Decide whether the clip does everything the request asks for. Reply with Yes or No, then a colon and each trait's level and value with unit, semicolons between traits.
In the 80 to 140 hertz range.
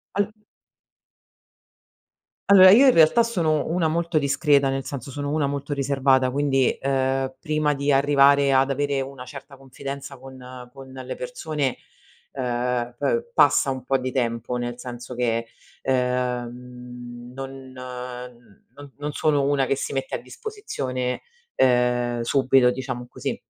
Yes: low, 135 Hz